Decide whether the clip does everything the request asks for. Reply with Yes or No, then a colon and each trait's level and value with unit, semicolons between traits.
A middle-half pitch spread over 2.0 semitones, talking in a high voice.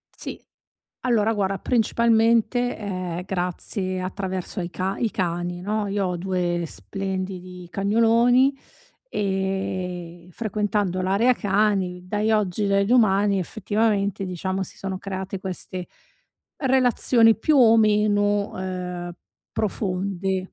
Yes: average, 2.7 semitones; high, 195 Hz